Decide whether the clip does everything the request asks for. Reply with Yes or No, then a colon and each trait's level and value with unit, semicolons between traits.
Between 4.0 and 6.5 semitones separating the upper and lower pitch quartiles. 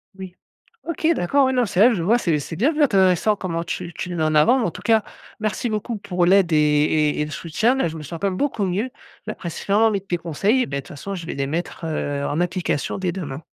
Yes: average, 5.2 semitones